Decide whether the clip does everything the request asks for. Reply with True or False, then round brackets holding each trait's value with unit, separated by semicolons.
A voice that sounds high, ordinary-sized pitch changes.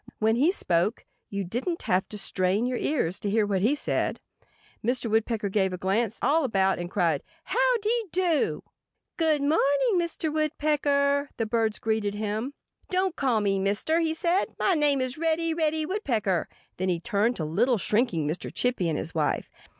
False (235 Hz; 7.6 semitones)